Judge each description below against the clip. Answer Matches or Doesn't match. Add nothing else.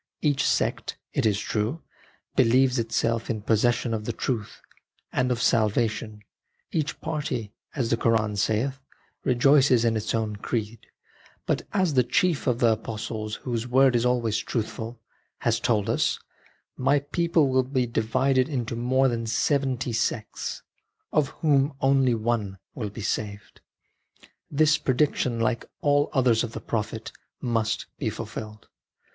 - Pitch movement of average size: Matches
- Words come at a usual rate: Matches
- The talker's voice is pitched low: Matches